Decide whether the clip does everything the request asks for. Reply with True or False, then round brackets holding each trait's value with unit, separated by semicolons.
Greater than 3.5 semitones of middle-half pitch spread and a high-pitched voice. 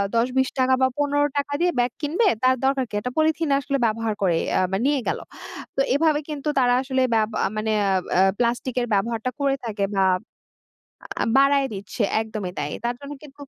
True (4.3 semitones; 260 Hz)